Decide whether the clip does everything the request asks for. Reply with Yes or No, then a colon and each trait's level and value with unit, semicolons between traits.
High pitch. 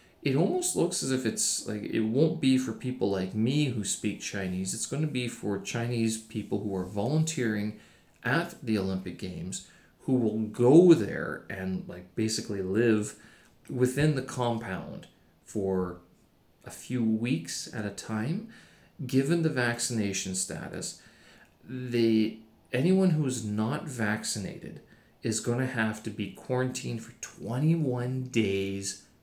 No: low, 115 Hz